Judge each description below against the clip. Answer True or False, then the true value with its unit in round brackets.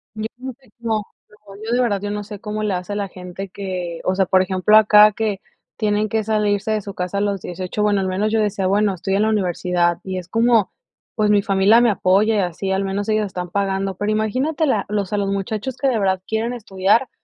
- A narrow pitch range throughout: True (2.1 semitones)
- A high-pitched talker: True (205 Hz)